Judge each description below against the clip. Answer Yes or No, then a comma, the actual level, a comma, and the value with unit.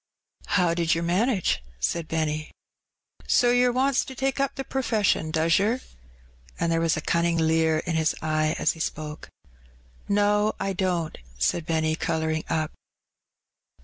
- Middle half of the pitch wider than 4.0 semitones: Yes, average, 4.6 semitones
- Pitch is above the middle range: No, medium, 165 Hz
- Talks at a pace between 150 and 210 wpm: Yes, average, 155 wpm